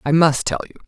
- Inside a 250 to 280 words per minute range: Yes, fast, 275 wpm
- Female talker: Yes, female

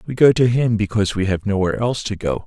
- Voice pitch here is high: No, low, 105 Hz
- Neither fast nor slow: No, fast, 270 wpm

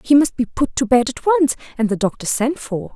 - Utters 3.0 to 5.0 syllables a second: No, 5.4 syllables/s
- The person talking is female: Yes, female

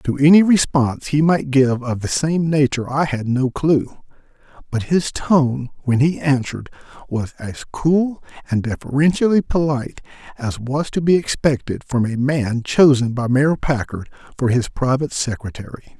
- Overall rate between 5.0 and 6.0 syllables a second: No, 4.8 syllables/s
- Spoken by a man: Yes, male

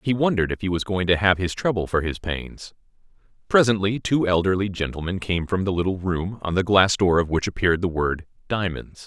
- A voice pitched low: Yes, very low, 95 Hz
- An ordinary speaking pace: No, fast, 210 wpm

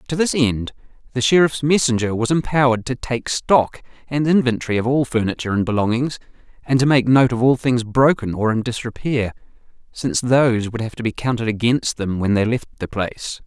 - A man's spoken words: Yes, male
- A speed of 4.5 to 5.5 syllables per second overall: No, 5.7 syllables/s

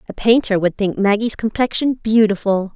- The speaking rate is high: No, average, 150 wpm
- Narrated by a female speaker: Yes, female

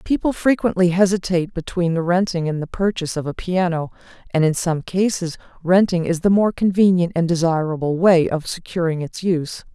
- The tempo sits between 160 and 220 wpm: Yes, average, 170 wpm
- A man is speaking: No, female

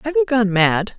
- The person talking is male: No, female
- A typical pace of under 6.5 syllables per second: Yes, 4.8 syllables/s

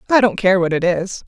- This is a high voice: Yes, high, 195 Hz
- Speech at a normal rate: No, fast, 285 wpm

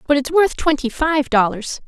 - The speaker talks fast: No, average, 190 wpm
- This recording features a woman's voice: Yes, female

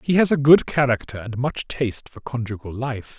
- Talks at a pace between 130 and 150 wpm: No, fast, 205 wpm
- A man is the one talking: Yes, male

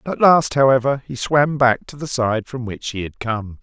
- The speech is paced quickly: Yes, fast, 230 wpm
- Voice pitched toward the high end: No, low, 130 Hz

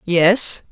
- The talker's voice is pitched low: No, high, 190 Hz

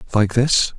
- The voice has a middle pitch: No, low, 115 Hz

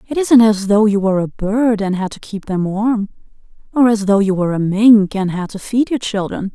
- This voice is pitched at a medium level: No, high, 210 Hz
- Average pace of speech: No, fast, 245 wpm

